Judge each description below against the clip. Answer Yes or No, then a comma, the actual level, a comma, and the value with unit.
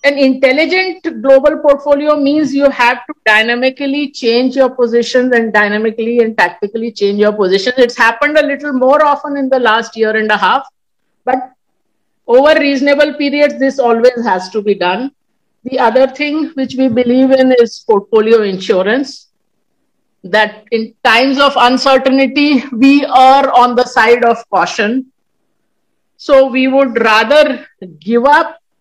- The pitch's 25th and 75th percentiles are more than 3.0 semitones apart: Yes, average, 3.5 semitones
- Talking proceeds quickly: No, average, 145 wpm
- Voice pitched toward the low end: No, very high, 255 Hz